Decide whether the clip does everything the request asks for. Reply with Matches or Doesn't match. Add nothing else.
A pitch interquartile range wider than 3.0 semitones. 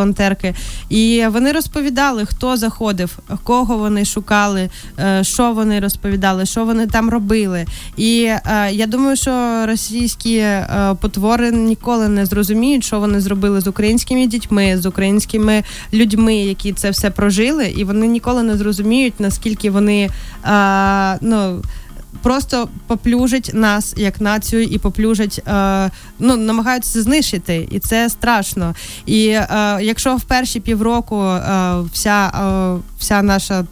Doesn't match